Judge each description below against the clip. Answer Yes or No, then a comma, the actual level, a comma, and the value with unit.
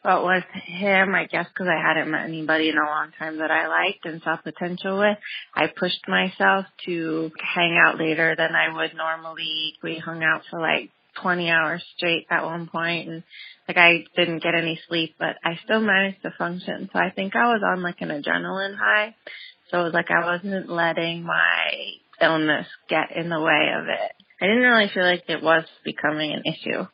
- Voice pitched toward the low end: No, medium, 170 Hz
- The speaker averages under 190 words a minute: No, fast, 205 wpm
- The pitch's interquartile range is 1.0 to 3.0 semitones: Yes, narrow, 2.4 semitones